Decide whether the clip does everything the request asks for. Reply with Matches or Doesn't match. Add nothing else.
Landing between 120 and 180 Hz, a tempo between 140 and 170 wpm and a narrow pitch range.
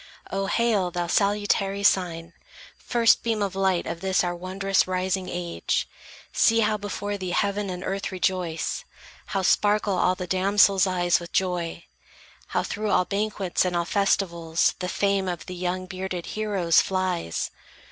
Doesn't match